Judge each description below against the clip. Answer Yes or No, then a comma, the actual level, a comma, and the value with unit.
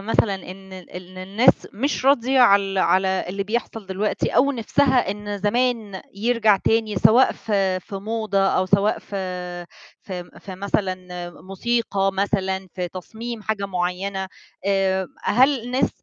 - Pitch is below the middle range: No, high, 200 Hz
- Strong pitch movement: No, average, 2.9 semitones